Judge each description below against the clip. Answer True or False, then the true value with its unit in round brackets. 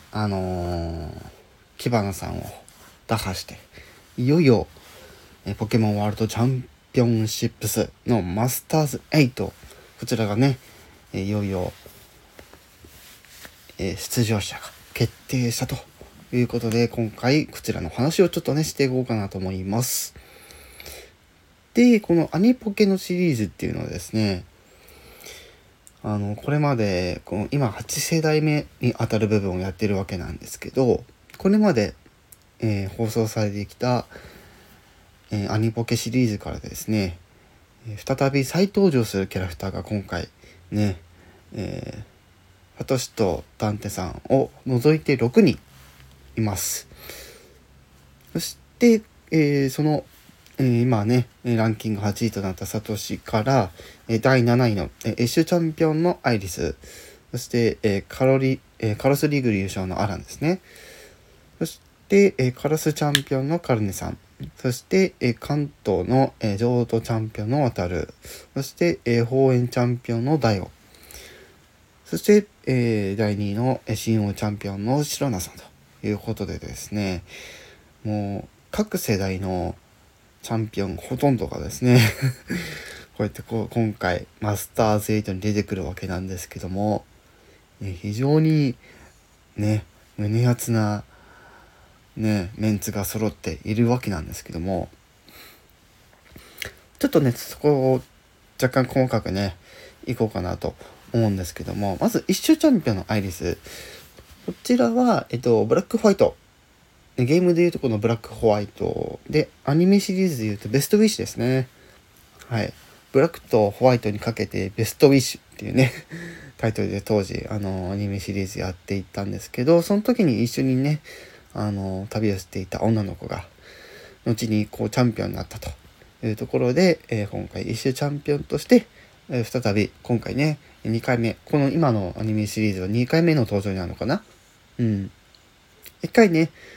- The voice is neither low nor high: False (110 Hz)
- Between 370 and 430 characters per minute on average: False (295 characters per minute)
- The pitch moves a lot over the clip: False (5.0 semitones)